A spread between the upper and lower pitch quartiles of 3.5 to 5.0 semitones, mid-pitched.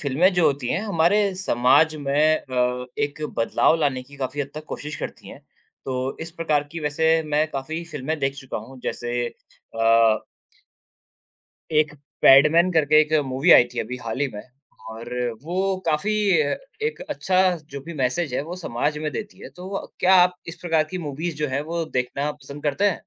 Yes: average, 3.8 semitones; medium, 150 Hz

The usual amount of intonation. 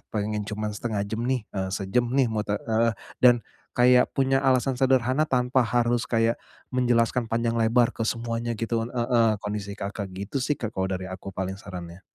Yes: average, 3.1 semitones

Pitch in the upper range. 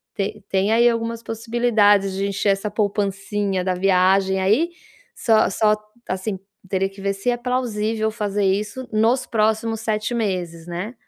Yes: high, 210 Hz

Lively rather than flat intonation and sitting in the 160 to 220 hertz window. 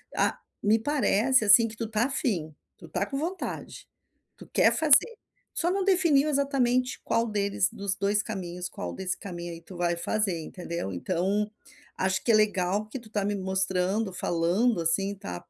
No: average, 4.9 semitones; high, 205 Hz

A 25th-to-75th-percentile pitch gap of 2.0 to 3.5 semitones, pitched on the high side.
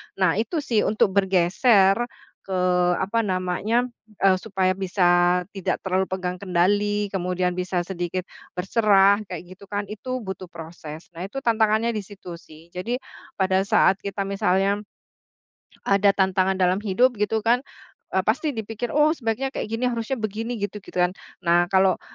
Yes: average, 3.1 semitones; high, 195 Hz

